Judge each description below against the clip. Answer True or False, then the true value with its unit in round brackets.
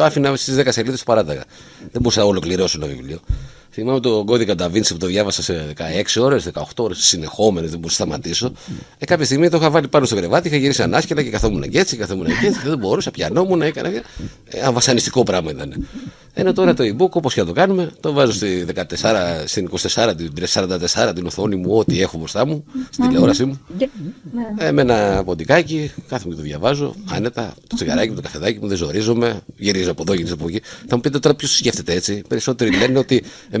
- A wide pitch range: True (8.2 semitones)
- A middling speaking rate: False (215 wpm)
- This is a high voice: False (115 Hz)